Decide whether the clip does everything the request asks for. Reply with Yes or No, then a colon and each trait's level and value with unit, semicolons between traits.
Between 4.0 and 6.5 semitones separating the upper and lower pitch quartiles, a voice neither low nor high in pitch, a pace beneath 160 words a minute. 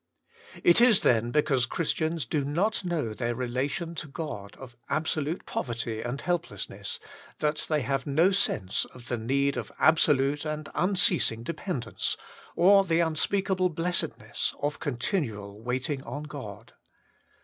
Yes: wide, 5.5 semitones; medium, 145 Hz; average, 140 wpm